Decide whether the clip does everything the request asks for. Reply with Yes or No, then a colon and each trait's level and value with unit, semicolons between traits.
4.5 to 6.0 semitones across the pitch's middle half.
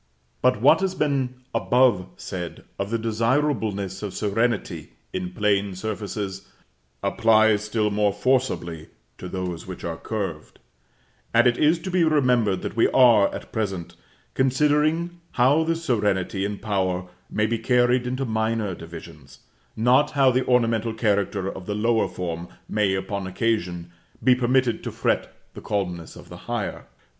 Yes: average, 4.8 semitones